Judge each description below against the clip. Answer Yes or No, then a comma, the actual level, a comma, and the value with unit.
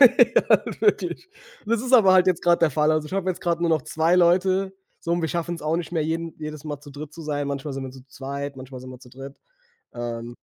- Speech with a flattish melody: No, average, 3.9 semitones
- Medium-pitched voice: Yes, medium, 155 Hz